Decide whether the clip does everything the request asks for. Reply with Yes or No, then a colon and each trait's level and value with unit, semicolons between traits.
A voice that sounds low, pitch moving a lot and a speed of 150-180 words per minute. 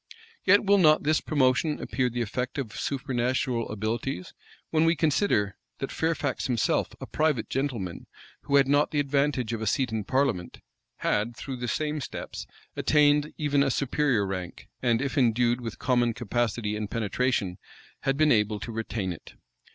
No: low, 125 Hz; average, 4.4 semitones; average, 165 wpm